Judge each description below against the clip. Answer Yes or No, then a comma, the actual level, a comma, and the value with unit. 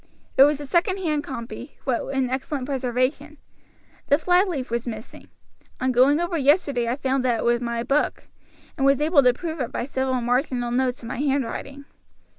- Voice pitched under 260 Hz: No, very high, 265 Hz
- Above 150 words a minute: Yes, average, 185 wpm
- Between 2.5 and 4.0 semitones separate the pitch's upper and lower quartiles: Yes, average, 2.9 semitones